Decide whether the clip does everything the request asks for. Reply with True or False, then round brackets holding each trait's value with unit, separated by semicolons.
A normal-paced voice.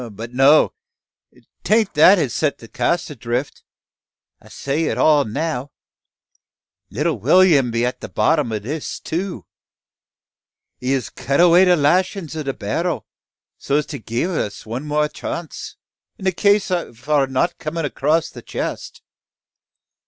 True (150 wpm)